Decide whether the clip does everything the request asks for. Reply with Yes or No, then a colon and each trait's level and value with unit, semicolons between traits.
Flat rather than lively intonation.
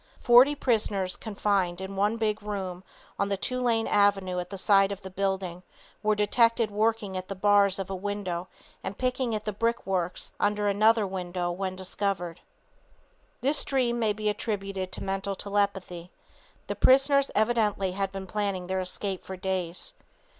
Yes: narrow, 2.3 semitones